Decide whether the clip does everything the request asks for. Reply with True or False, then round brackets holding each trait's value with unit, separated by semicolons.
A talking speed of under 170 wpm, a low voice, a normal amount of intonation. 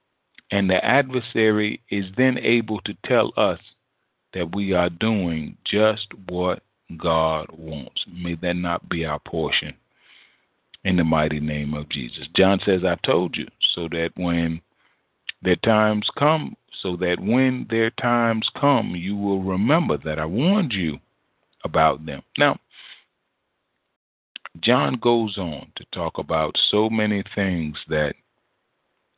True (135 wpm; 95 Hz; 4.6 semitones)